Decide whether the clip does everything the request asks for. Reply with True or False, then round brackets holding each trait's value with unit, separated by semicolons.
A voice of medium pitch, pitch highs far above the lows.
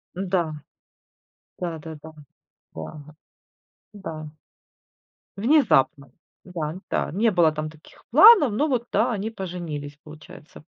True (175 Hz; 5.9 semitones)